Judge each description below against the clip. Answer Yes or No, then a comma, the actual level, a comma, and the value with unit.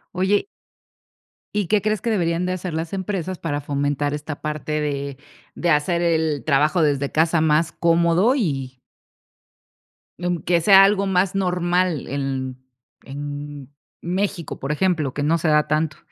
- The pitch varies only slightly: No, average, 3.8 semitones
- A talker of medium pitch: Yes, medium, 160 Hz